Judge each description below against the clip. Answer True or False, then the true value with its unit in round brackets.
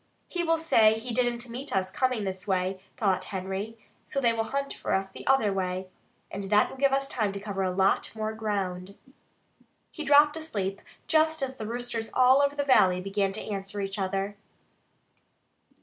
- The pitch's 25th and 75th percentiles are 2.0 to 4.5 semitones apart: False (5.1 semitones)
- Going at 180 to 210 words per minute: True (185 wpm)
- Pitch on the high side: True (215 Hz)